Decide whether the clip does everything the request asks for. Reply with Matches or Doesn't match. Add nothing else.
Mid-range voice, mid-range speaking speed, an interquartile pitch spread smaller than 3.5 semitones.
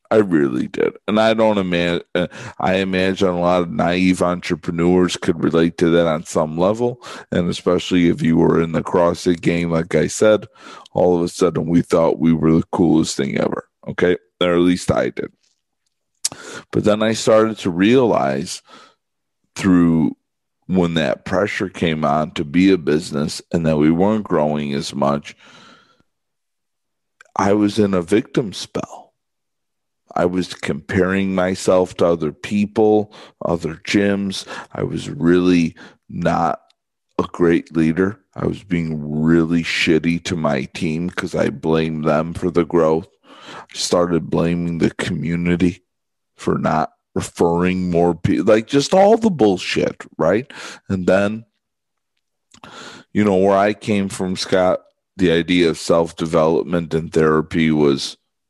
Doesn't match